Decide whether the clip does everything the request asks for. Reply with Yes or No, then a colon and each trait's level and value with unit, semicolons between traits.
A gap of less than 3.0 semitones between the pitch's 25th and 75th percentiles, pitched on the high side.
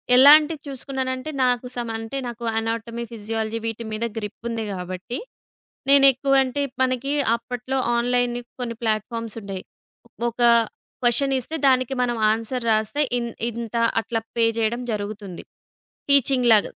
Yes: narrow, 2.6 semitones; high, 235 Hz